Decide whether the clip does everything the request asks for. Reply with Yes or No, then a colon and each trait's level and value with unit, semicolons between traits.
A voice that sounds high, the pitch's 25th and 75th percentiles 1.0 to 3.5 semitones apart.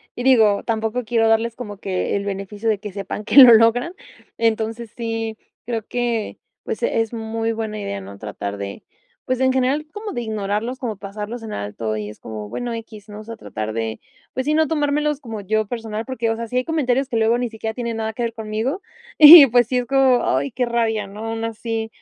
Yes: high, 225 Hz; average, 2.7 semitones